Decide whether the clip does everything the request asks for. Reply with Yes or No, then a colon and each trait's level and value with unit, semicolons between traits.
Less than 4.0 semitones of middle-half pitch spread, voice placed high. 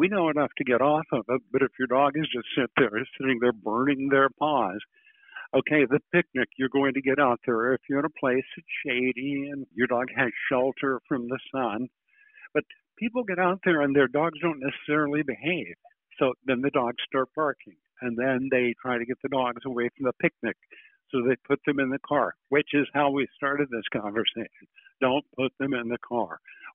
No: average, 2.7 semitones; low, 135 Hz